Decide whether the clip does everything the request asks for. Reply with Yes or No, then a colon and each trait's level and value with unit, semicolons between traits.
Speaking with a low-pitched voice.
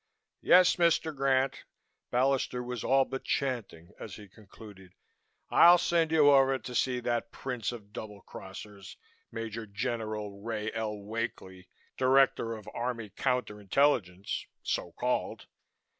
Yes: low, 115 Hz